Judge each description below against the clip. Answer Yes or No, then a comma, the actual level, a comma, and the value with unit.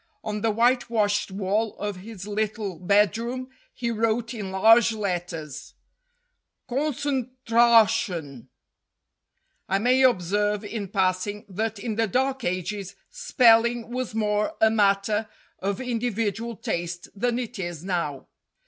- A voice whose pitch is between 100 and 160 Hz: No, high, 215 Hz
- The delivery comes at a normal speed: No, slow, 120 wpm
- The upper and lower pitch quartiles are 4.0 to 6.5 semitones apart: No, average, 3.2 semitones